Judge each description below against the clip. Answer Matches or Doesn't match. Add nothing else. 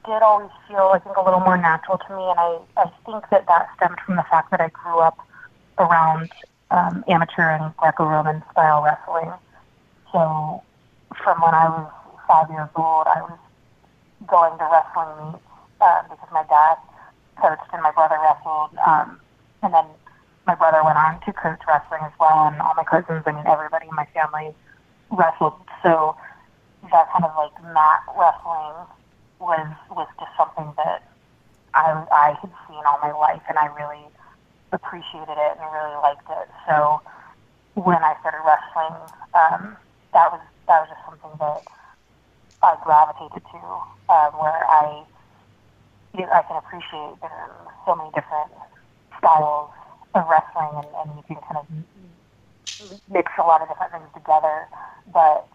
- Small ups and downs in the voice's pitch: Matches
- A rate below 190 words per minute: Matches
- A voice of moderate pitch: Matches